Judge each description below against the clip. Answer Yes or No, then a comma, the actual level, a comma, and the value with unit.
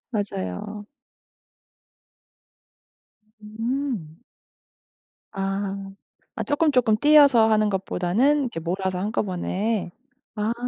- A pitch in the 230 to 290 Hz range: No, high, 210 Hz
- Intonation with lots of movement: No, average, 4.3 semitones